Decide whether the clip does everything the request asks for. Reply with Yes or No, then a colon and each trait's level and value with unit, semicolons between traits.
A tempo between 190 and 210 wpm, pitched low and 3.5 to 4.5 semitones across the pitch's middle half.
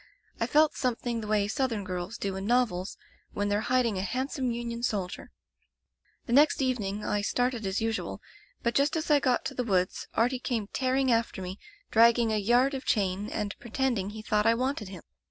No: average, 195 wpm; high, 230 Hz; average, 3.9 semitones